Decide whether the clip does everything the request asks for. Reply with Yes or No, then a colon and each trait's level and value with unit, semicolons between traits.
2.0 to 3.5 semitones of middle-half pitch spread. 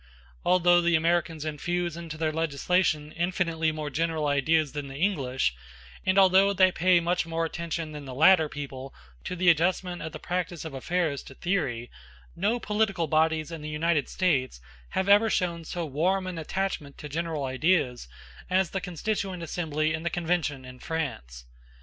Yes: average, 3.2 semitones